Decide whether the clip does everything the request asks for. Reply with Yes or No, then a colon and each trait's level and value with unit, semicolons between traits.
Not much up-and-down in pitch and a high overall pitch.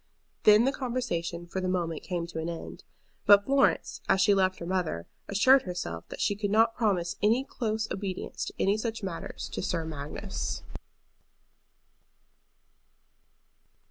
No: average, 4.2 semitones; high, 195 Hz